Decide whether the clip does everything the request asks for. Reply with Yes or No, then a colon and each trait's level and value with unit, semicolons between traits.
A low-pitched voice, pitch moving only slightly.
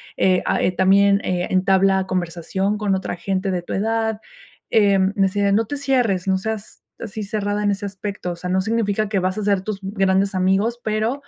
No: high, 195 Hz; narrow, 2.1 semitones